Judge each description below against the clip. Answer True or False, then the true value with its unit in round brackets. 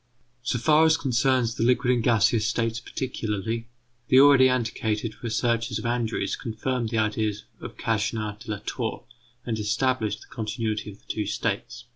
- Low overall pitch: True (115 Hz)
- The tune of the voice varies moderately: False (2.3 semitones)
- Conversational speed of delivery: True (160 wpm)